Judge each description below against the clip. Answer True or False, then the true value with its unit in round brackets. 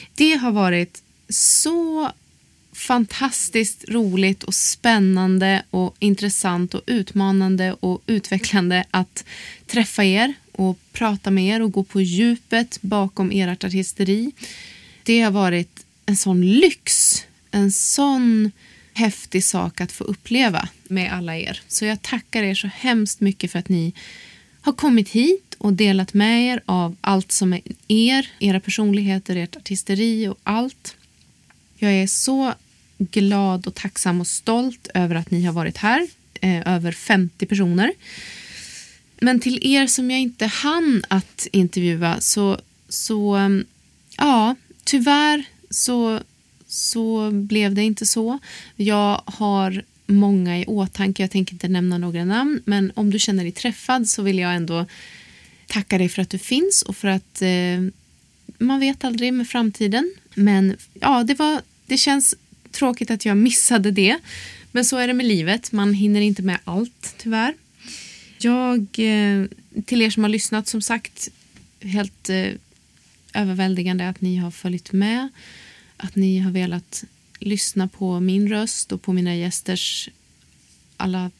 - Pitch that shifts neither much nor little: True (3.5 semitones)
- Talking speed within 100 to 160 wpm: True (145 wpm)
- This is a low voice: False (205 Hz)